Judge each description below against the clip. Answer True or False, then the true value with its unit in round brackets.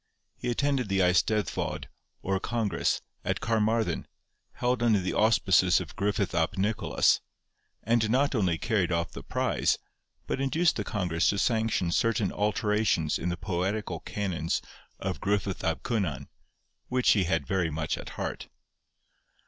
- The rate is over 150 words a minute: False (140 wpm)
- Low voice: True (100 Hz)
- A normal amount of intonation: True (4.2 semitones)